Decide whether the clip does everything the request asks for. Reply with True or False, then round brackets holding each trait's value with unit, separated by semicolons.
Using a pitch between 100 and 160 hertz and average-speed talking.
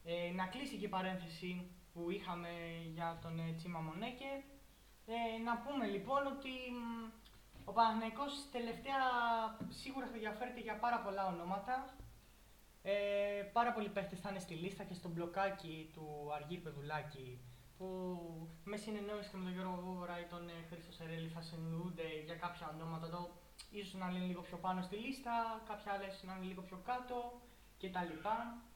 False (185 Hz; 160 wpm)